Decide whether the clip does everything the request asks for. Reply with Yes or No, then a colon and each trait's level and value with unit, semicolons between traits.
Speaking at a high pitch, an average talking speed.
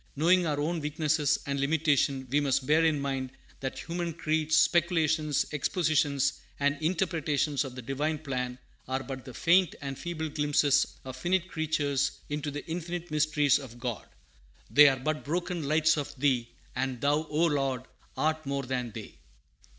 No: medium, 150 Hz; average, 160 wpm